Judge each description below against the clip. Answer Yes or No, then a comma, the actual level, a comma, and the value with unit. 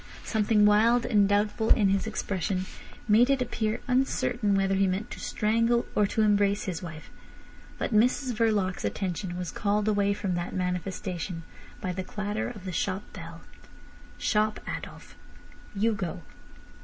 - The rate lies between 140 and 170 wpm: Yes, average, 150 wpm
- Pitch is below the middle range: No, high, 205 Hz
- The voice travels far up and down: No, average, 2.7 semitones